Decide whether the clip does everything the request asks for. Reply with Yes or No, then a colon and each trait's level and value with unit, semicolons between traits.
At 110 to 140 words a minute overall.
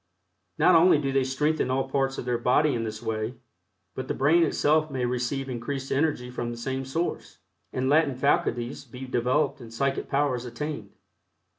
No: average, 175 wpm